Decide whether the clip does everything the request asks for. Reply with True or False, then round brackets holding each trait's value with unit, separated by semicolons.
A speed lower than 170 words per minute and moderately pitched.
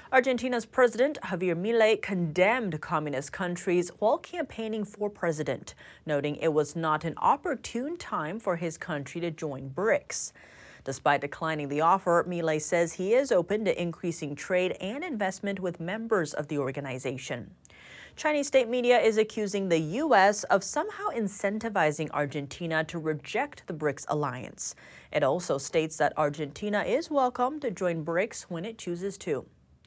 True (145 wpm; 180 Hz)